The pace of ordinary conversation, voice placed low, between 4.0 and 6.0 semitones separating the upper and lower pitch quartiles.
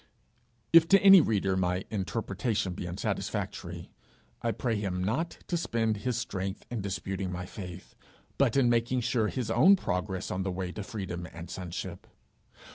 Yes: average, 160 wpm; low, 100 Hz; average, 4.6 semitones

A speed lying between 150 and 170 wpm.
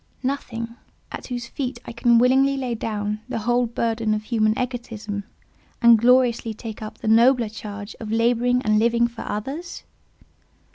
Yes: average, 155 wpm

